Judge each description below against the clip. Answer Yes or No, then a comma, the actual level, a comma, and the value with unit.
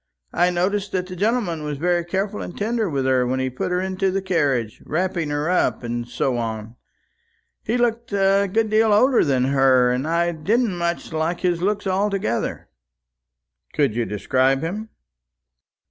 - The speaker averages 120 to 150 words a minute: No, average, 170 wpm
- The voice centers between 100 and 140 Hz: No, medium, 175 Hz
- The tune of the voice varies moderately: No, wide, 6.8 semitones